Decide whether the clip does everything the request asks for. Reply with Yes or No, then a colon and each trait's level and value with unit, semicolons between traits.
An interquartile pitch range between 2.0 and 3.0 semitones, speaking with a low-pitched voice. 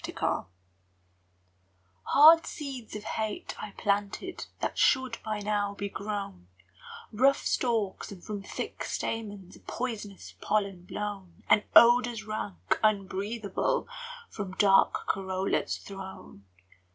No: narrow, 2.4 semitones; high, 205 Hz